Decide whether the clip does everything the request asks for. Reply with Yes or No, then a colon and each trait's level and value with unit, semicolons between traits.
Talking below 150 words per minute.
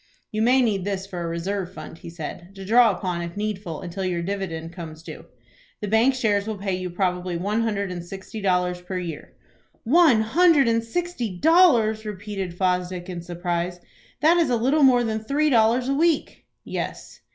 No: average, 185 wpm